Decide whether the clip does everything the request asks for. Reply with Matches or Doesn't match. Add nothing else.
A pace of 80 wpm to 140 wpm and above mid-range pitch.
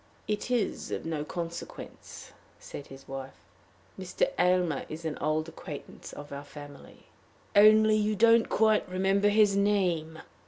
Doesn't match